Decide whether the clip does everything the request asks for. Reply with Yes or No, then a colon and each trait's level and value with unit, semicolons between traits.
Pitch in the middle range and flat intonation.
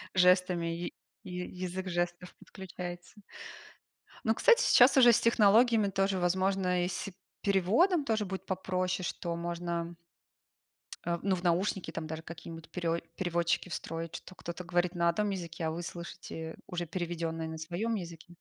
Yes: medium, 180 Hz; narrow, 2.1 semitones